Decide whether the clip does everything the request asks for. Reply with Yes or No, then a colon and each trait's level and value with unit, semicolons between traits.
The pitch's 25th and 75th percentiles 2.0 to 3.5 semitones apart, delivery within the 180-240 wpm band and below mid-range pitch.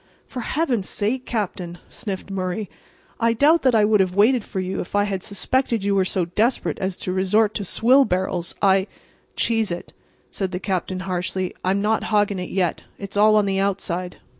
No: average, 2.8 semitones; average, 190 wpm; high, 200 Hz